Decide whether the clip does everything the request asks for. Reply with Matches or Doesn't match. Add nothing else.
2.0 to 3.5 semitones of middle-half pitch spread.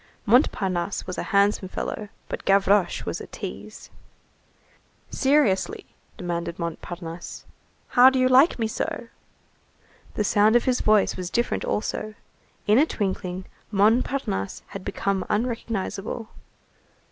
Doesn't match